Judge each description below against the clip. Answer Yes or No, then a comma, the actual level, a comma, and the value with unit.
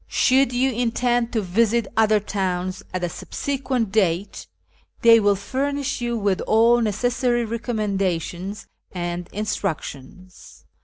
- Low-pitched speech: No, high, 215 Hz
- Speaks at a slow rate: Yes, slow, 115 wpm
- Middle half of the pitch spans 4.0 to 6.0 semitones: Yes, average, 4.3 semitones